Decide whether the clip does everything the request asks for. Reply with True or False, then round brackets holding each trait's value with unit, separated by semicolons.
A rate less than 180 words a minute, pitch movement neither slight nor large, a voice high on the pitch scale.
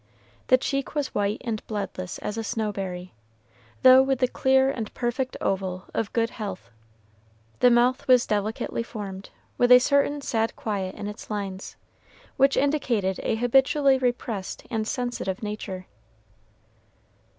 True (140 wpm; 4.2 semitones; 225 Hz)